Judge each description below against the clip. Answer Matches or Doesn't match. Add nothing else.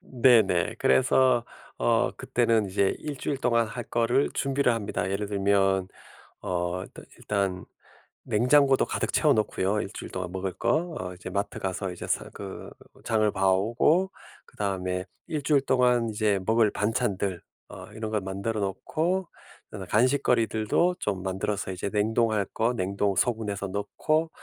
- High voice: Doesn't match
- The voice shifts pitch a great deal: Doesn't match